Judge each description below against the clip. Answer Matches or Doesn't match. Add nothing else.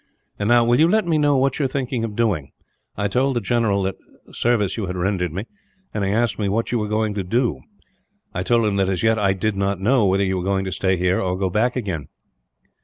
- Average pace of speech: Doesn't match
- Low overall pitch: Matches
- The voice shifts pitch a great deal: Doesn't match